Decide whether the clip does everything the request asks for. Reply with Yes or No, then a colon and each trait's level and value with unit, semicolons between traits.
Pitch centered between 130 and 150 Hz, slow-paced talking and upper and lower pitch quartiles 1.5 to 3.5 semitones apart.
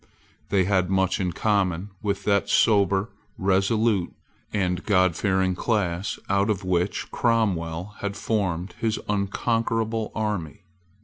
No: low, 100 Hz; slow, 115 wpm; narrow, 2.6 semitones